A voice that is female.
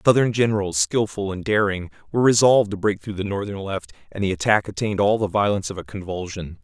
No: male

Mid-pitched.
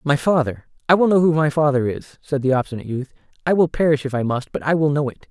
Yes: medium, 145 Hz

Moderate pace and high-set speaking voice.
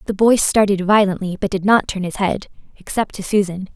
Yes: average, 190 wpm; high, 195 Hz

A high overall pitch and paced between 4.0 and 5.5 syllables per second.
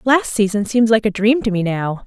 Yes: high, 215 Hz; 5.1 syllables/s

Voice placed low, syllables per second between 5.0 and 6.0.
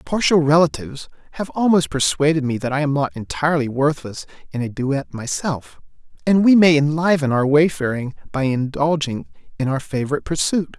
No: medium, 145 Hz; 5.4 syllables/s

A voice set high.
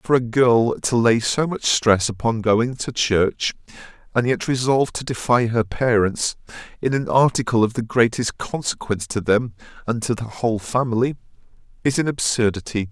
No: low, 120 Hz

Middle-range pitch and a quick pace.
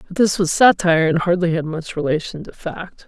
Yes: medium, 170 Hz; fast, 215 wpm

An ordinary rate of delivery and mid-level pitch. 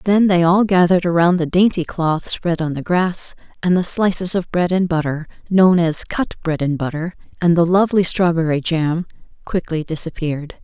Yes: average, 180 wpm; medium, 170 Hz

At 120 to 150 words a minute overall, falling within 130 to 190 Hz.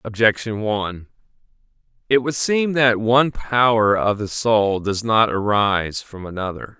No: average, 140 wpm; low, 110 Hz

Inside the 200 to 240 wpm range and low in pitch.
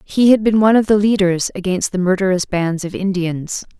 No: fast, 205 wpm; high, 190 Hz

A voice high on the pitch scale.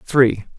No: low, 125 Hz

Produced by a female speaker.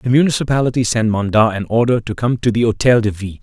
No: male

